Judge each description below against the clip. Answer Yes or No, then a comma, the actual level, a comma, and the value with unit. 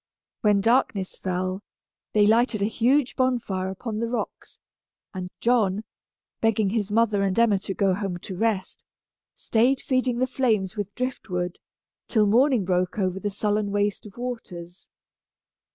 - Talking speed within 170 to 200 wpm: No, average, 150 wpm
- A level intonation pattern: No, average, 3.6 semitones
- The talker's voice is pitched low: No, high, 210 Hz